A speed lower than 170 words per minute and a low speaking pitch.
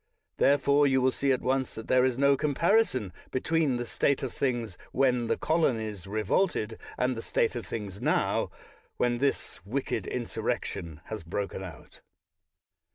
Yes: average, 160 wpm; low, 125 Hz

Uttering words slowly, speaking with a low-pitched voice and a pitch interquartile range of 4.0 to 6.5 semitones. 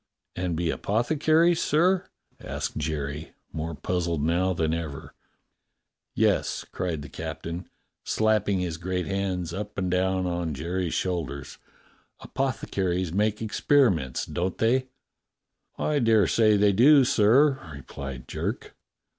Yes: slow, 120 wpm; very low, 95 Hz; average, 4.9 semitones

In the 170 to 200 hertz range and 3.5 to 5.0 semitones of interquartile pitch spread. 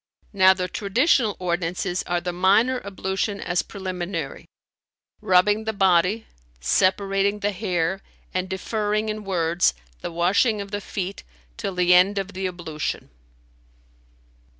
No: high, 190 Hz; narrow, 2.4 semitones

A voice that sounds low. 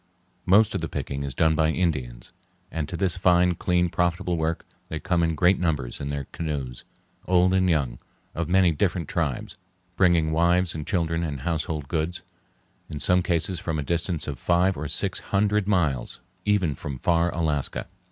Yes: very low, 85 Hz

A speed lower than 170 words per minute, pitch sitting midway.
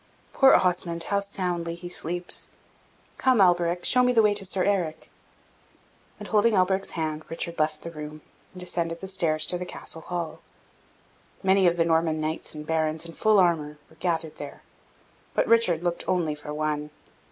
No: average, 175 wpm; medium, 170 Hz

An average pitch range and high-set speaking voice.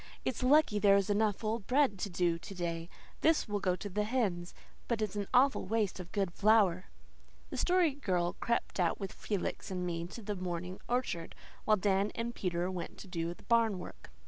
Yes: average, 4.0 semitones; high, 200 Hz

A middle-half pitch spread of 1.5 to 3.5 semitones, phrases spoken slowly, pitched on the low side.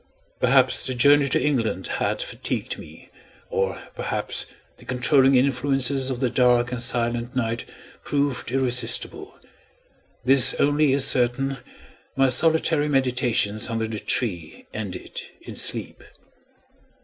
Yes: narrow, 2.4 semitones; slow, 120 wpm; low, 125 Hz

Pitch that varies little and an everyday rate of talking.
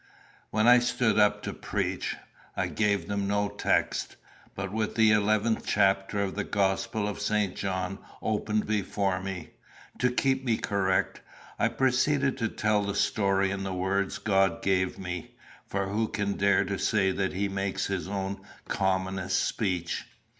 Yes: narrow, 1.8 semitones; average, 160 wpm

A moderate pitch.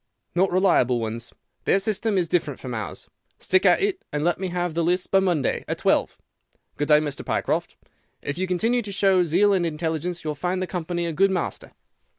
Yes: medium, 175 Hz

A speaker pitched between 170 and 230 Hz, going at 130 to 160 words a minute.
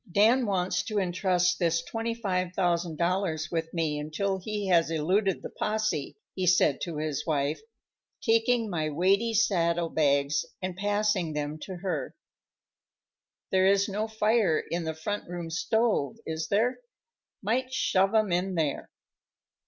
Yes: medium, 185 Hz; slow, 135 wpm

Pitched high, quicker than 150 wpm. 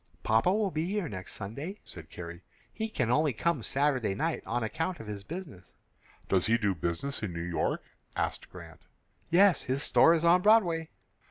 No: medium, 140 Hz; average, 180 wpm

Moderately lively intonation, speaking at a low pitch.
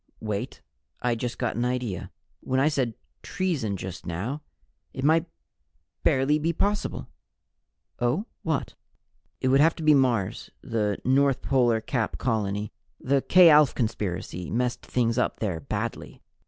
Yes: average, 4.5 semitones; low, 125 Hz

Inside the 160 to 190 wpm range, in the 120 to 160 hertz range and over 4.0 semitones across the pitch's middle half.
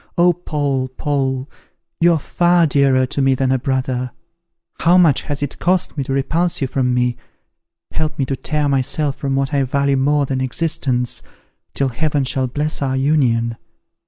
No: average, 175 wpm; low, 135 Hz; narrow, 2.4 semitones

